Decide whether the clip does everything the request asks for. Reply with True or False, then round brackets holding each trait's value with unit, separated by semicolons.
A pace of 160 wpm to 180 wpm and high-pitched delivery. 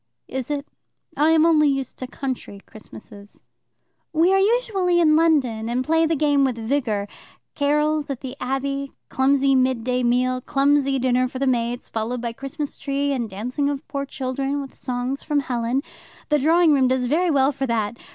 True (175 wpm; 270 Hz)